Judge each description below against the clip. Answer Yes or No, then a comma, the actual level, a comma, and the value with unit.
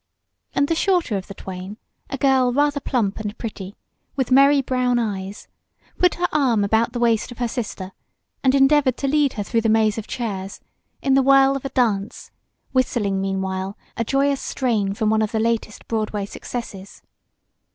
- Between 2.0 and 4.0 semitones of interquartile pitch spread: No, average, 4.7 semitones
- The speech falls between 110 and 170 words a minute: No, average, 180 wpm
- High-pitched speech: Yes, high, 230 Hz